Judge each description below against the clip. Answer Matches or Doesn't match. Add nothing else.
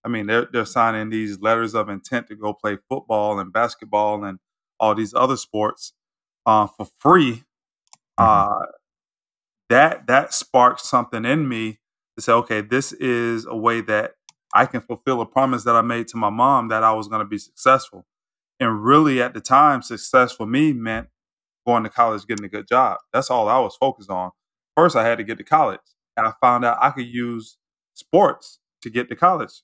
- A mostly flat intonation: Matches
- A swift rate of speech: Doesn't match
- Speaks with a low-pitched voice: Matches